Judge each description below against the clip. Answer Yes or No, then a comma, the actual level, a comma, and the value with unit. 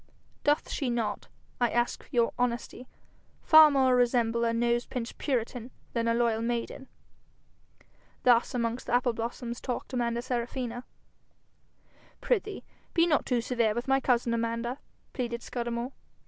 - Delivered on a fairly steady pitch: Yes, narrow, 1.4 semitones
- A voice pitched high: Yes, high, 240 Hz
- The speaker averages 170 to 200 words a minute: No, slow, 135 wpm